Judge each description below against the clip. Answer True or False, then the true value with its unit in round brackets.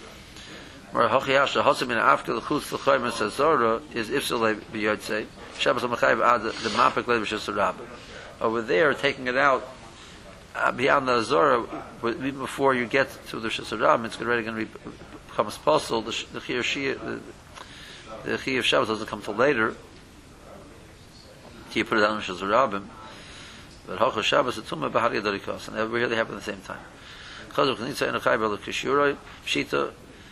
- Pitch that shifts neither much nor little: False (2.1 semitones)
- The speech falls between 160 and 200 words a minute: True (165 wpm)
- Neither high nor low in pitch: False (110 Hz)